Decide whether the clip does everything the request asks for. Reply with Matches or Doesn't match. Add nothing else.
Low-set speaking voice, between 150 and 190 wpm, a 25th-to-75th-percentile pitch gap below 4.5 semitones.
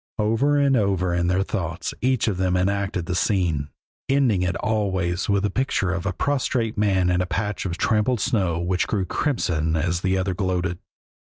Matches